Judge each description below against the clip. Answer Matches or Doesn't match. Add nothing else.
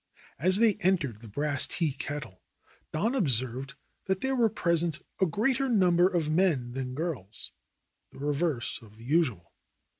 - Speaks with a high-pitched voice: Doesn't match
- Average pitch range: Doesn't match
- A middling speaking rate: Matches